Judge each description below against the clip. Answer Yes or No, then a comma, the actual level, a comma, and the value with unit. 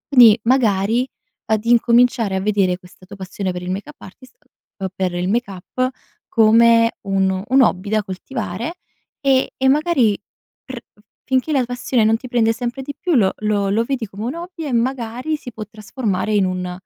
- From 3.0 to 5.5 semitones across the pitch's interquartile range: Yes, average, 4.5 semitones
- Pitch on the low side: No, high, 225 Hz